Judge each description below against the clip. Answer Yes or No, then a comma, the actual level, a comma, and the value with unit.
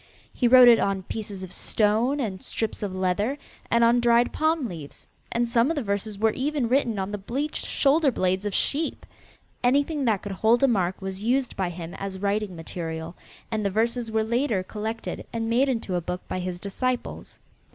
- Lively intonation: No, average, 4.3 semitones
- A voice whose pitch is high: Yes, high, 220 Hz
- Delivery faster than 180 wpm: Yes, average, 195 wpm